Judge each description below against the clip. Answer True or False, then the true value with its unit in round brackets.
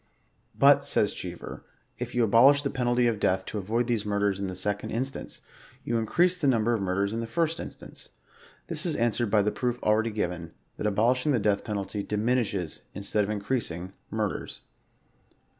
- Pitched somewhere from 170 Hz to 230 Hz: False (110 Hz)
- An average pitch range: True (3.4 semitones)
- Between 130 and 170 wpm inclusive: False (185 wpm)